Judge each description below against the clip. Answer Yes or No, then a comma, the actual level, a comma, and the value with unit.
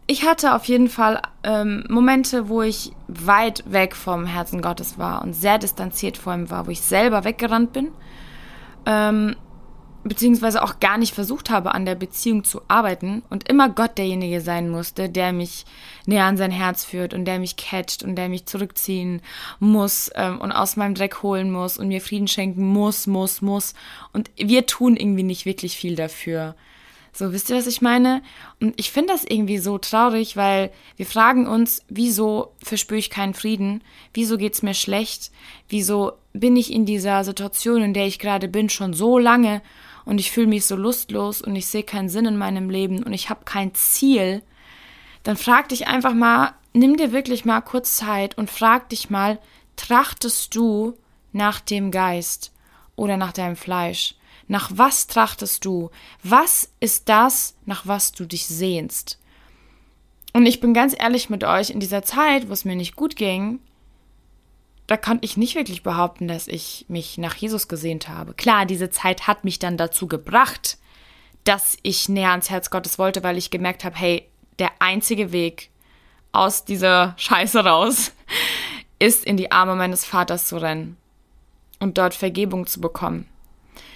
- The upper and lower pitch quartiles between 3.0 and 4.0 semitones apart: Yes, average, 3.5 semitones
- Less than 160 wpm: No, average, 175 wpm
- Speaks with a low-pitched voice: No, high, 200 Hz